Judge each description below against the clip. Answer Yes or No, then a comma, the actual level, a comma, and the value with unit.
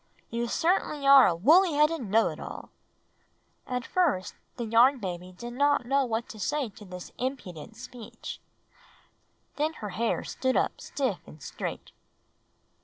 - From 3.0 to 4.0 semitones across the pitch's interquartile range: No, average, 5.3 semitones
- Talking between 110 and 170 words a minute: Yes, average, 150 wpm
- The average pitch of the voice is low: No, high, 240 Hz